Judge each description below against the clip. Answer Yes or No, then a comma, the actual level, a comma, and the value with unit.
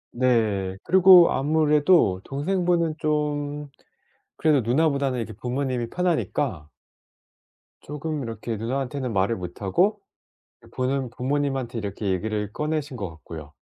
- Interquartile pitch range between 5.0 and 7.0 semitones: Yes, wide, 5.4 semitones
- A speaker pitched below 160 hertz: Yes, low, 135 Hz